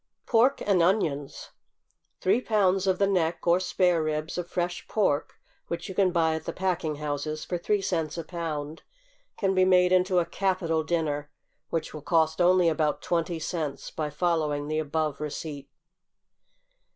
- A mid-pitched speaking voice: Yes, medium, 170 Hz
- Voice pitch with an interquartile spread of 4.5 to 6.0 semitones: No, average, 3.1 semitones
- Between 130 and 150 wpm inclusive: No, average, 165 wpm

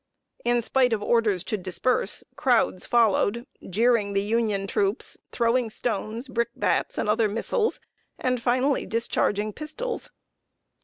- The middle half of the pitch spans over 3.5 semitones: No, average, 3.2 semitones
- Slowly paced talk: Yes, slow, 120 wpm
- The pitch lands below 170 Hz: No, high, 230 Hz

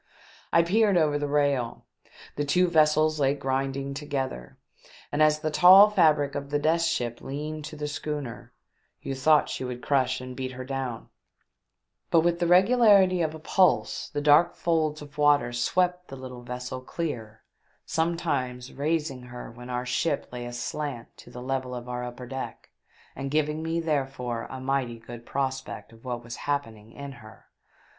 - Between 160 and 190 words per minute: Yes, average, 170 wpm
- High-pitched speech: No, medium, 140 Hz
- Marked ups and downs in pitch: No, average, 3.7 semitones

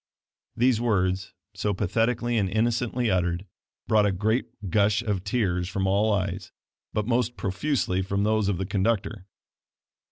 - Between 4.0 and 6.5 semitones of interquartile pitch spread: No, average, 3.2 semitones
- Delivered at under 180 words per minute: Yes, average, 140 wpm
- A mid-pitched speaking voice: No, low, 105 Hz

